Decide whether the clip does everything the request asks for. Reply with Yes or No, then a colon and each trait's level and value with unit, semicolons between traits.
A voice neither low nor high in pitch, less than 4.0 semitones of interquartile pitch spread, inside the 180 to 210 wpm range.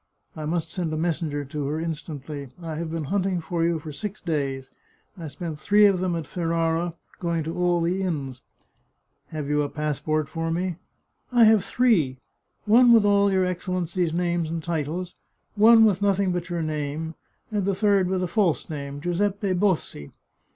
Yes: medium, 170 Hz; average, 3.4 semitones; average, 190 wpm